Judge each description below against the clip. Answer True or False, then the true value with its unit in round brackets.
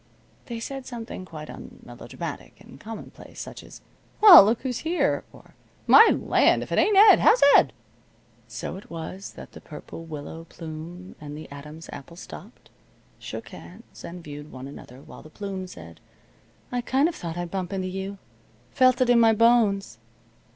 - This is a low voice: False (185 Hz)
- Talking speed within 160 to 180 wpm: True (170 wpm)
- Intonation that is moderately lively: False (7.1 semitones)